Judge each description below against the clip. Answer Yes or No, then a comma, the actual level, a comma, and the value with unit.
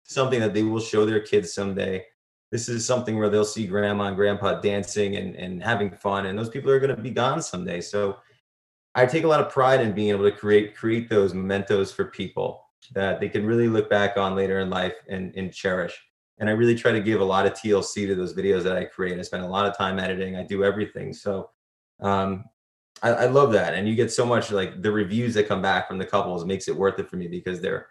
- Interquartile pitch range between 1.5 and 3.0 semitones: Yes, average, 2.7 semitones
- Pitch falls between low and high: No, low, 100 Hz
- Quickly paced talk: Yes, fast, 245 wpm